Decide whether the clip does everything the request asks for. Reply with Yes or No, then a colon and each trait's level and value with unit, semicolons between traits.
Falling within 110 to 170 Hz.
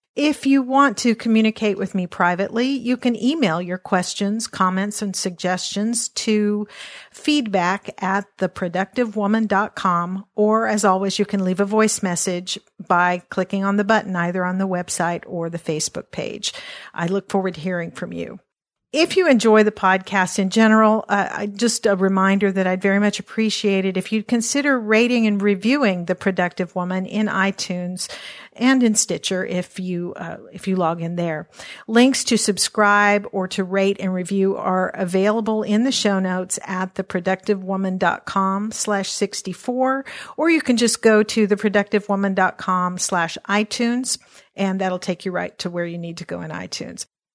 No: high, 200 Hz